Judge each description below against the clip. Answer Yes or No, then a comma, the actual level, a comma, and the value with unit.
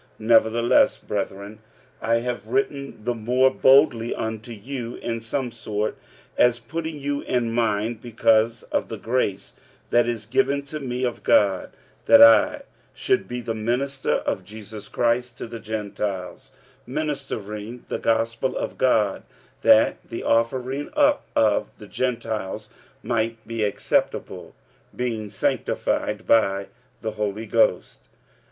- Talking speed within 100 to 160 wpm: Yes, slow, 135 wpm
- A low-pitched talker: Yes, low, 115 Hz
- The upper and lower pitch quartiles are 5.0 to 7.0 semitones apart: No, average, 2.9 semitones